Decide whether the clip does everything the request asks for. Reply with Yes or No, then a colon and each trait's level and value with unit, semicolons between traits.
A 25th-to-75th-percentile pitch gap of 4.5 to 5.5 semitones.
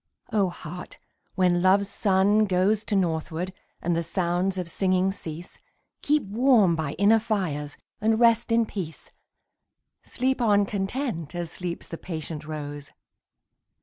No: average, 4.0 semitones